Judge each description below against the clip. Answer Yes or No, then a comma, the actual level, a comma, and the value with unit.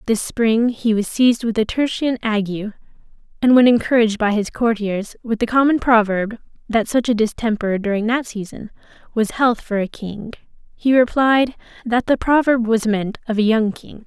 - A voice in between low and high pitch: No, high, 225 Hz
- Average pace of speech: Yes, average, 180 wpm